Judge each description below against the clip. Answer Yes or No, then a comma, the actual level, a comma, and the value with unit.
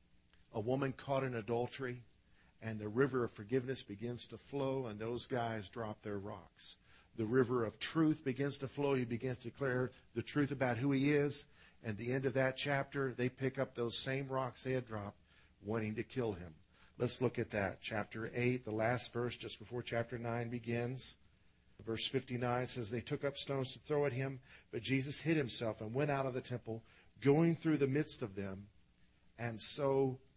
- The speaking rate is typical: Yes, average, 195 wpm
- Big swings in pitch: No, average, 3.2 semitones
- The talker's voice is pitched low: Yes, low, 125 Hz